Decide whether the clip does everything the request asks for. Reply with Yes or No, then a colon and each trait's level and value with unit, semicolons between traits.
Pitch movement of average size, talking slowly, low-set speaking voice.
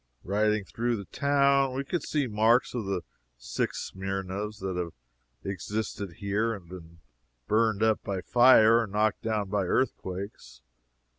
No: average, 3.1 semitones; average, 145 wpm; low, 105 Hz